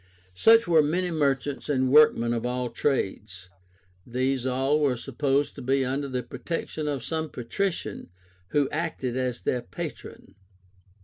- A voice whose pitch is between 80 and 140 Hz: Yes, low, 135 Hz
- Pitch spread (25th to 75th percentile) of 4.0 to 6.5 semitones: No, average, 3.2 semitones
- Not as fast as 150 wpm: Yes, average, 140 wpm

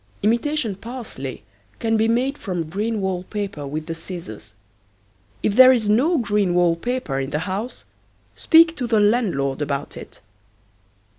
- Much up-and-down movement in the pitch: Yes, wide, 6.5 semitones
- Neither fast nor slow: Yes, average, 150 wpm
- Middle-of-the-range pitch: No, high, 205 Hz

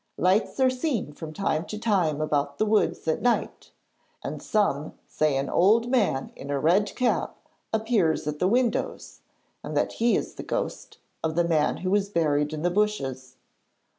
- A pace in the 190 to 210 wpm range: No, average, 175 wpm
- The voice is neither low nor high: Yes, medium, 180 Hz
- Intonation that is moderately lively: No, wide, 6.1 semitones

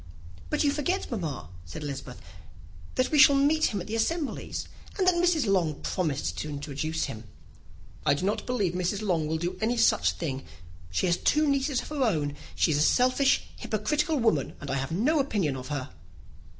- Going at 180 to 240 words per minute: Yes, average, 195 wpm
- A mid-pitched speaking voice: No, high, 195 Hz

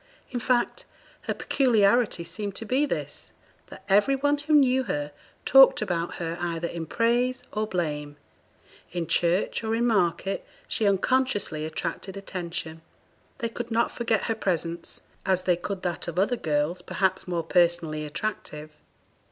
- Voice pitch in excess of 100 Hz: Yes, high, 190 Hz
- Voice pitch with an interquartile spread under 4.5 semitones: No, wide, 5.6 semitones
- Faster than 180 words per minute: No, average, 150 wpm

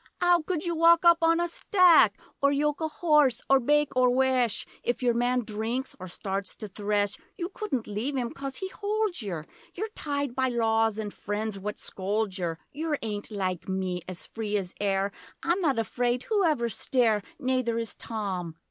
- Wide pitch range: Yes, wide, 6.4 semitones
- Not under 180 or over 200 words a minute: Yes, average, 185 wpm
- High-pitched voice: Yes, high, 245 Hz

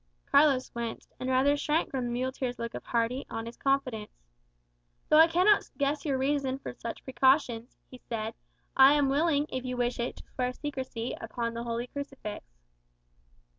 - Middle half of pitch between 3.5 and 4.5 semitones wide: No, average, 2.9 semitones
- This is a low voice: No, very high, 260 Hz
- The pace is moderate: Yes, average, 170 wpm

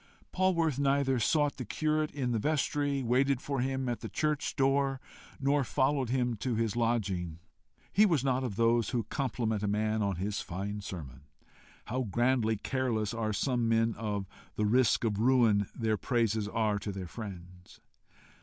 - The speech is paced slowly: No, average, 165 wpm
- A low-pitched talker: Yes, low, 115 Hz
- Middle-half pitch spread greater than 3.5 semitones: Yes, average, 4.2 semitones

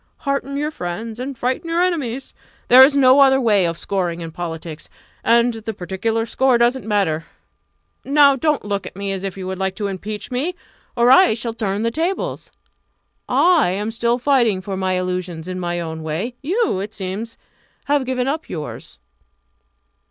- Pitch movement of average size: No, wide, 6.0 semitones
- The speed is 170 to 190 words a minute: Yes, average, 175 wpm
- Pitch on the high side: Yes, high, 225 Hz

